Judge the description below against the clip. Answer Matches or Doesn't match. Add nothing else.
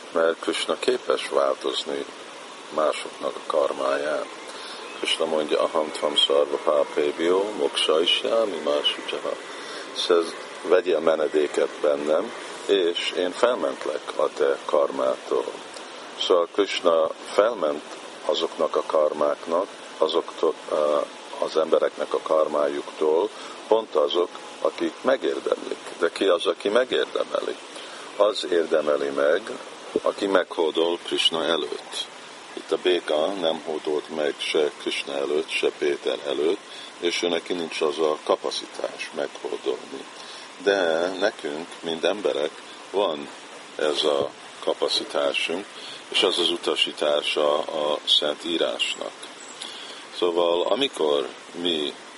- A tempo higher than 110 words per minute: Doesn't match